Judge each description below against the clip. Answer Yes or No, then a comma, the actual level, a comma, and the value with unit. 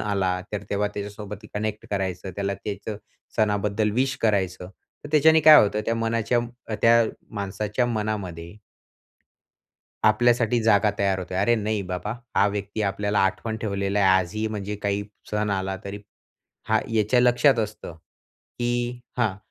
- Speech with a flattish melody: Yes, narrow, 2.3 semitones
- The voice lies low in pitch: Yes, low, 105 Hz